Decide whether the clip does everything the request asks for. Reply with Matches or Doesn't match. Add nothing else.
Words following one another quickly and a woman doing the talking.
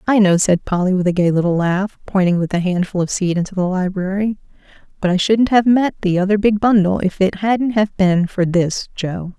Matches